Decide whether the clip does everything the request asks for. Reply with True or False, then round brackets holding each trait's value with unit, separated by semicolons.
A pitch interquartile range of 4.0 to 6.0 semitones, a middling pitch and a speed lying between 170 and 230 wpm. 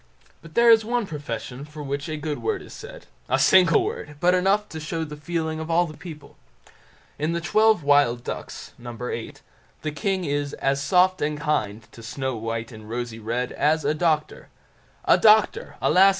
True (4.9 semitones; 150 Hz; 180 wpm)